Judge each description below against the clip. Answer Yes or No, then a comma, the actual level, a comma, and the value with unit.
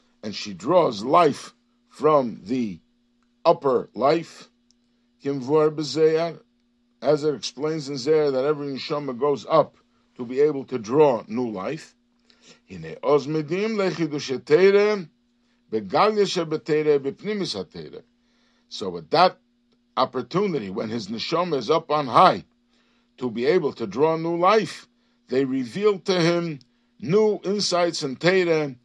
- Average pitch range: No, wide, 7.4 semitones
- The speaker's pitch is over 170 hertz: No, medium, 160 Hz